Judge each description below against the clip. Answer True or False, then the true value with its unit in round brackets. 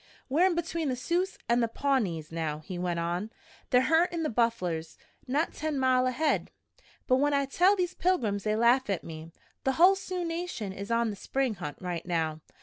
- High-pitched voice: True (250 Hz)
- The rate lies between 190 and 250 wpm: True (195 wpm)